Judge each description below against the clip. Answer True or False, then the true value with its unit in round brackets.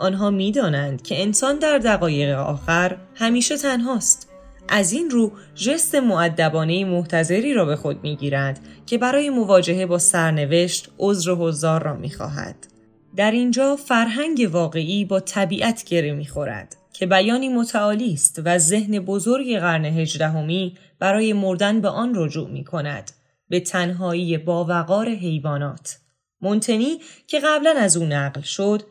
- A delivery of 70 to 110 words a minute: False (140 wpm)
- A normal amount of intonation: False (6.1 semitones)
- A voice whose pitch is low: False (185 Hz)